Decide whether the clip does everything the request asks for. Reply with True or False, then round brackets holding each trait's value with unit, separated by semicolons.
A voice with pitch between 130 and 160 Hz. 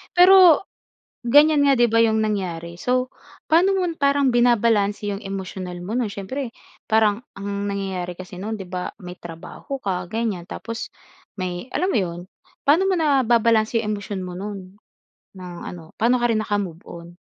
False (210 Hz)